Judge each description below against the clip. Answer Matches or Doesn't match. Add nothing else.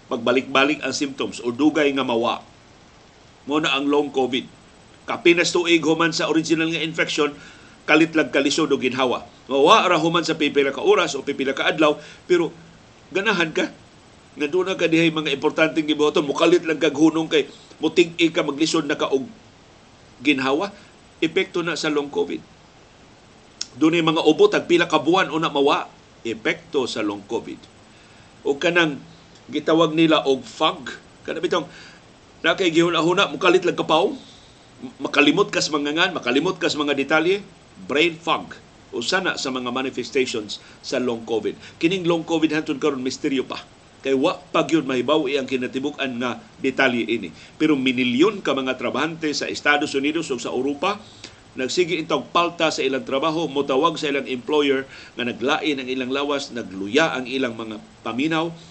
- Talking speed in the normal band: Doesn't match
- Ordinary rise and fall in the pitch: Matches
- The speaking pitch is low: Doesn't match